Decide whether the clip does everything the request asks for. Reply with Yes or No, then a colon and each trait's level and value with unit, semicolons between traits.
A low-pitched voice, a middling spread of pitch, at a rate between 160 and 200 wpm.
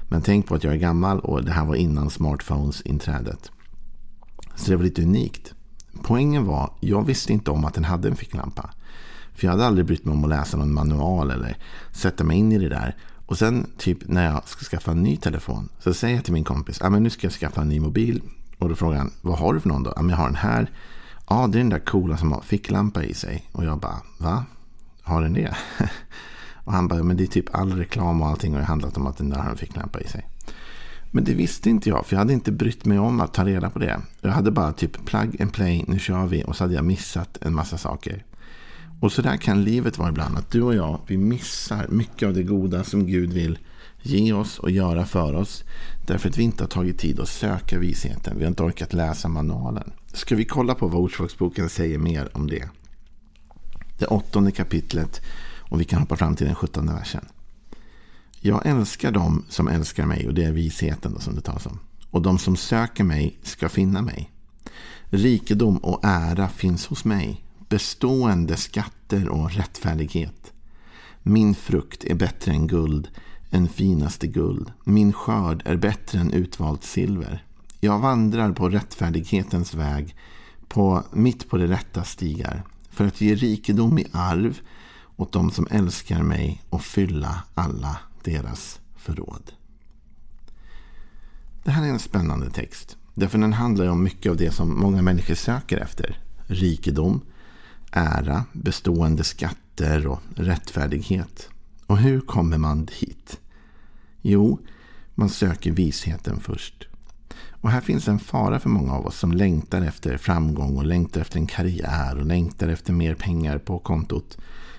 Yes: very low, 90 Hz; average, 4.3 semitones; average, 190 wpm